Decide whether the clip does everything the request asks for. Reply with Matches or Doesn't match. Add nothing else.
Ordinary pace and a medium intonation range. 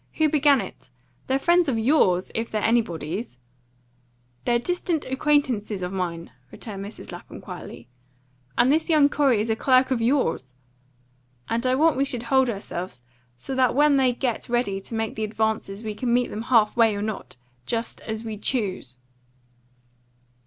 Matches